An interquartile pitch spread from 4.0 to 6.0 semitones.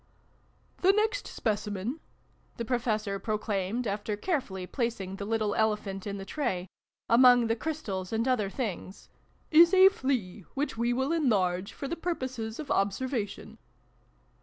Yes: average, 4.8 semitones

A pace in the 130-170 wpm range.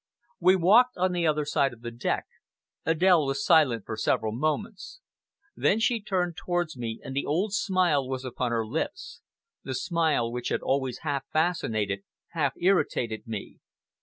Yes: average, 165 wpm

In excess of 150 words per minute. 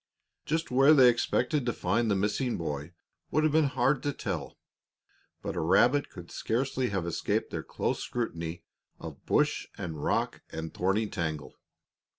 Yes: average, 160 wpm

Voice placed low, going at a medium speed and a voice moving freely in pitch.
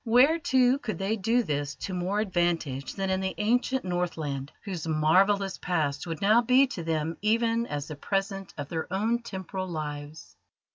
No: high, 190 Hz; average, 175 wpm; wide, 5.8 semitones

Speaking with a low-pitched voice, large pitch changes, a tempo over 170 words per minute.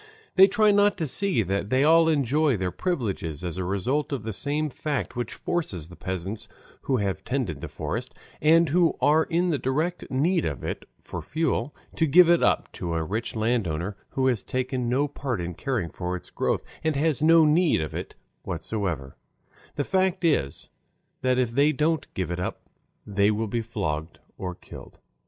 Yes: low, 130 Hz; wide, 8.5 semitones; average, 190 wpm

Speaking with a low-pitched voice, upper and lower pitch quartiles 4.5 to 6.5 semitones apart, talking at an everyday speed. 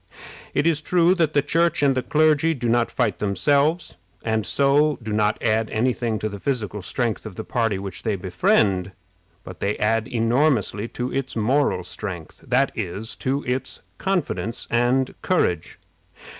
Yes: low, 120 Hz; average, 5.3 semitones; average, 165 wpm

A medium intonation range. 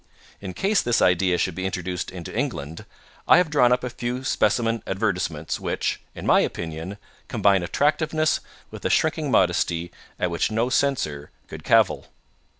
No: wide, 6.6 semitones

